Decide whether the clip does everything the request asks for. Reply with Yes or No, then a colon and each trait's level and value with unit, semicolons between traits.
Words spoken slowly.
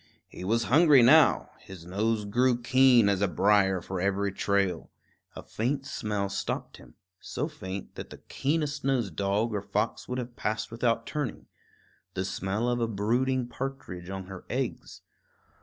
No: average, 160 wpm